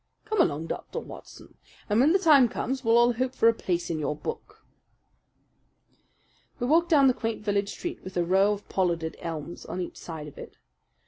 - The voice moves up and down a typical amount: No, wide, 7.0 semitones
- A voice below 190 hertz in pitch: No, high, 210 Hz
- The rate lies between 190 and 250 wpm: Yes, average, 195 wpm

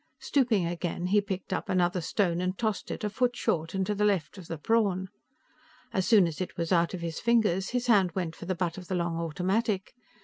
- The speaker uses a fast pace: Yes, fast, 230 wpm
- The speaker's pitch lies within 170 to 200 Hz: Yes, medium, 185 Hz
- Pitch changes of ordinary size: Yes, average, 3.3 semitones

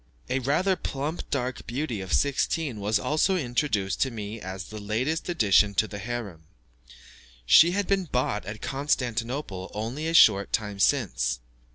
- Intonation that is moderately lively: No, wide, 6.0 semitones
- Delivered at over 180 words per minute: No, average, 155 wpm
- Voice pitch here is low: Yes, low, 120 Hz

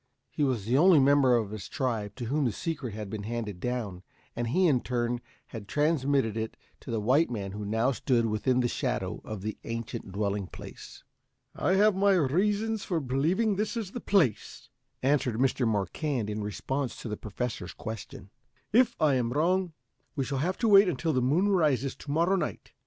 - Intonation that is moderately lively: No, wide, 6.7 semitones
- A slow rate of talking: No, average, 190 wpm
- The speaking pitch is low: Yes, low, 130 Hz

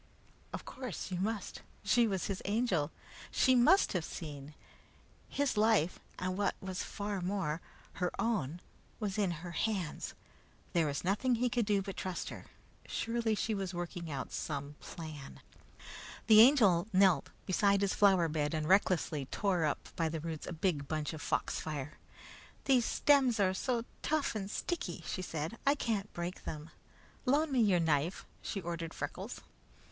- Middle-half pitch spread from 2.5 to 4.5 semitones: No, average, 5.0 semitones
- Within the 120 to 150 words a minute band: No, average, 160 wpm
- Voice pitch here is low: No, high, 190 Hz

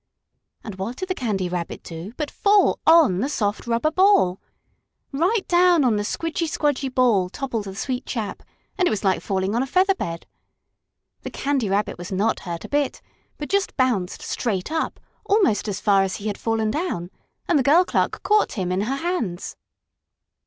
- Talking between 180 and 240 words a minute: Yes, average, 190 wpm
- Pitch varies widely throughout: Yes, wide, 8.7 semitones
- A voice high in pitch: Yes, high, 240 Hz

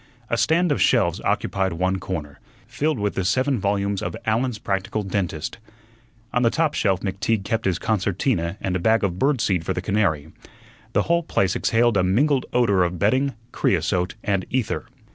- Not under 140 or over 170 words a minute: No, average, 180 wpm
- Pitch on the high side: No, low, 100 Hz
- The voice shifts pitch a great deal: No, average, 4.4 semitones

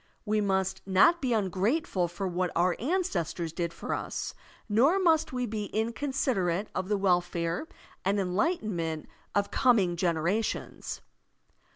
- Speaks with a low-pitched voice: No, high, 195 Hz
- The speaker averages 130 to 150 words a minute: Yes, average, 140 wpm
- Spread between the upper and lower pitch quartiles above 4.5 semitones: Yes, average, 5.0 semitones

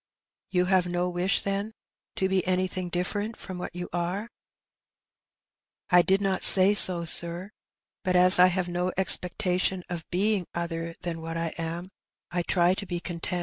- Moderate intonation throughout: No, narrow, 1.5 semitones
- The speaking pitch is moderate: Yes, medium, 180 Hz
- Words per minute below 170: No, average, 175 wpm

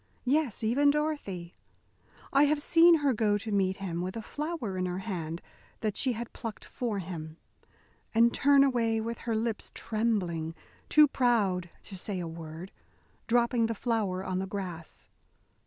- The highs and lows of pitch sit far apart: No, average, 4.9 semitones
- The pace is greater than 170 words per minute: No, average, 160 wpm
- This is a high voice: Yes, high, 220 Hz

